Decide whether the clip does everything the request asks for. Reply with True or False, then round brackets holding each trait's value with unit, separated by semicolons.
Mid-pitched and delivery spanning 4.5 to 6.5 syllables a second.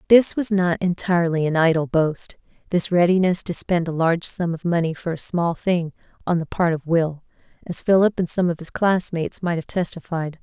True (170 Hz; 5.3 syllables/s)